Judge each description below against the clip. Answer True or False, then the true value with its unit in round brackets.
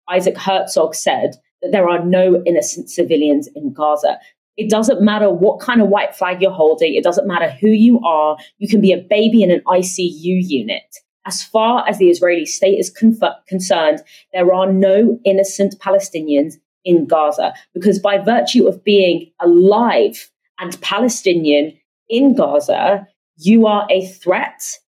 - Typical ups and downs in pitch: True (3.5 semitones)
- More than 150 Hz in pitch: True (190 Hz)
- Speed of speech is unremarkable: True (160 wpm)